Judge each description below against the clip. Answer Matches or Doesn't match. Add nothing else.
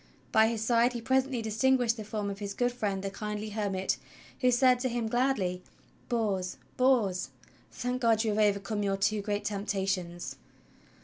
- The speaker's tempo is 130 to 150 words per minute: Doesn't match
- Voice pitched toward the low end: Doesn't match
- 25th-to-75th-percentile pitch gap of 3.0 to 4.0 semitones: Matches